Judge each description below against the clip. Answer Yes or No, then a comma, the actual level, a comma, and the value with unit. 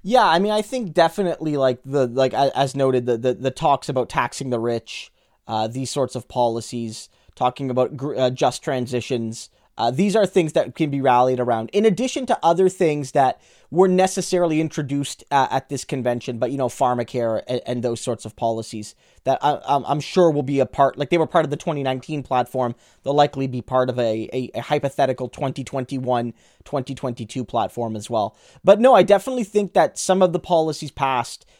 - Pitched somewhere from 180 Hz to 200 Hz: No, low, 135 Hz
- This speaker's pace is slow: No, average, 195 wpm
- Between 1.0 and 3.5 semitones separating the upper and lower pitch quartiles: No, average, 4.5 semitones